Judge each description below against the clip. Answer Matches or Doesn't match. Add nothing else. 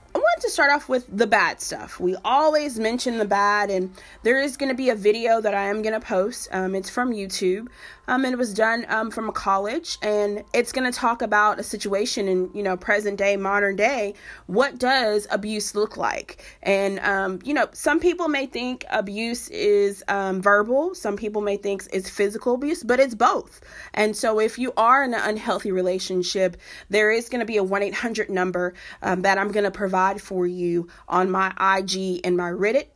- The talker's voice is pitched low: Doesn't match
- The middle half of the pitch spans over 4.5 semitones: Doesn't match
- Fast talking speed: Matches